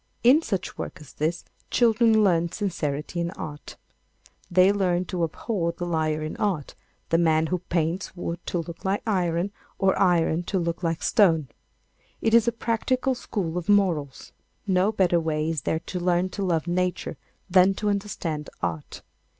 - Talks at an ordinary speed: Yes, average, 165 wpm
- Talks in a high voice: No, medium, 175 Hz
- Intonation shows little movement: No, average, 3.4 semitones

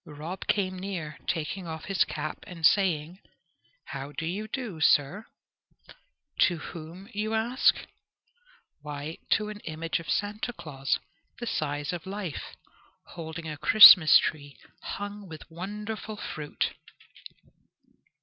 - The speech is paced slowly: Yes, slow, 120 wpm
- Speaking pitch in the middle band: Yes, medium, 175 Hz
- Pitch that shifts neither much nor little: Yes, average, 4.8 semitones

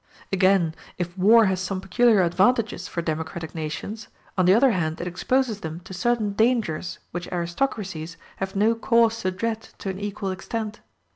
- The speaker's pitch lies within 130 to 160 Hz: No, high, 190 Hz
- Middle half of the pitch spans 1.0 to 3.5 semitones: No, average, 4.2 semitones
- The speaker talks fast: No, average, 165 wpm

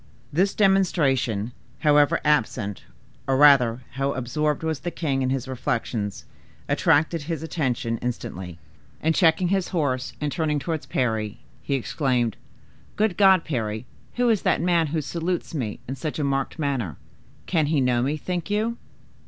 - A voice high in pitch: No, medium, 145 Hz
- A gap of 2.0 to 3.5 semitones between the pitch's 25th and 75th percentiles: No, average, 4.9 semitones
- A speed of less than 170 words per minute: Yes, average, 155 wpm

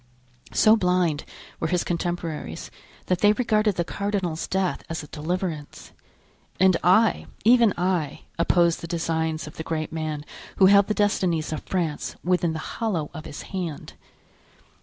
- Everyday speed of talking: Yes, average, 150 wpm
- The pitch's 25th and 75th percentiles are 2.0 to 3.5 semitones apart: Yes, average, 3.1 semitones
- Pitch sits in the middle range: Yes, medium, 175 Hz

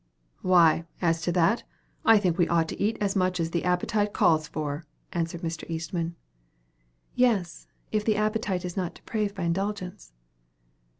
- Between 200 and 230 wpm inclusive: No, average, 160 wpm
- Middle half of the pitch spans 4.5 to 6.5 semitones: No, average, 3.6 semitones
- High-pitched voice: No, medium, 180 Hz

